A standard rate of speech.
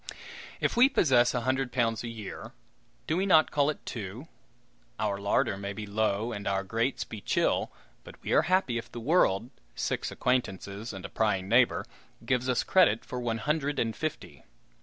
Yes: average, 180 wpm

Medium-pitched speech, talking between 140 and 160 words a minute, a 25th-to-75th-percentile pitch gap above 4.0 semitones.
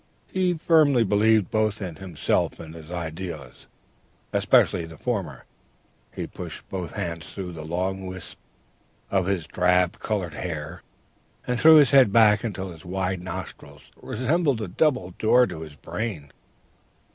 No: very low, 95 Hz; average, 145 wpm; average, 4.7 semitones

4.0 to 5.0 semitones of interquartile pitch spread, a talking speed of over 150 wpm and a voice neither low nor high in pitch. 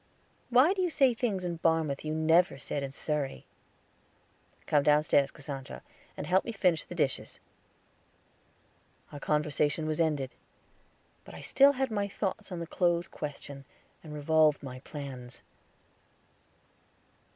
No: average, 4.5 semitones; slow, 135 wpm; medium, 155 Hz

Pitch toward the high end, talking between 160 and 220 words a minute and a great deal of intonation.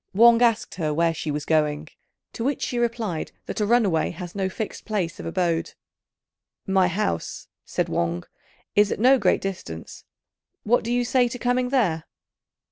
Yes: high, 195 Hz; average, 170 wpm; wide, 6.5 semitones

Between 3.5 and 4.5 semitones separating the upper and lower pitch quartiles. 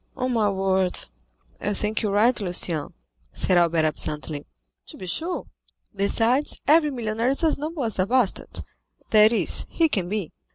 No: wide, 5.5 semitones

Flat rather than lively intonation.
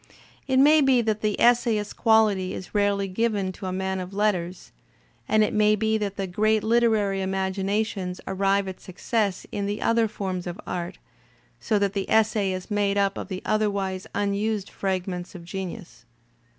Yes: narrow, 2.3 semitones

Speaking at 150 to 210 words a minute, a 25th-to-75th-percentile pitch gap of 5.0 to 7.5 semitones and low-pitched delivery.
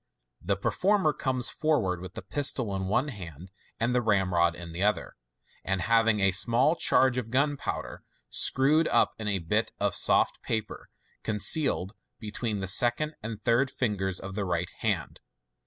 Yes: average, 165 wpm; average, 5.3 semitones; low, 110 Hz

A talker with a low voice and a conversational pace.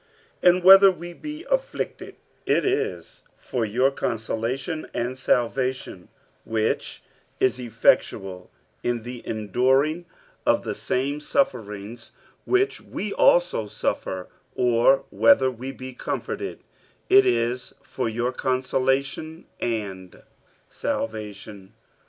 No: low, 125 Hz; slow, 105 wpm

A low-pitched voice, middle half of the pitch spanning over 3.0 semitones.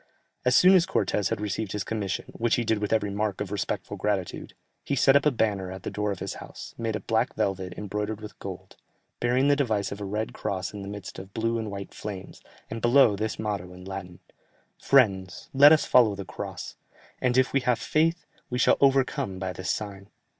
Yes: low, 105 Hz; average, 3.7 semitones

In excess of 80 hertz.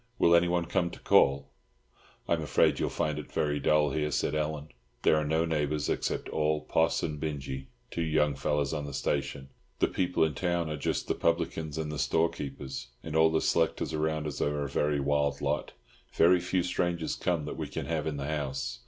No: very low, 75 Hz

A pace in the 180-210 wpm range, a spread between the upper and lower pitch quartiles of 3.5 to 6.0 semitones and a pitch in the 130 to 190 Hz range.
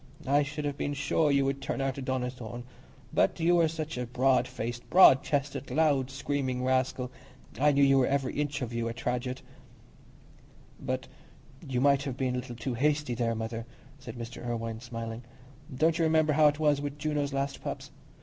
No: average, 190 wpm; average, 2.8 semitones; low, 135 Hz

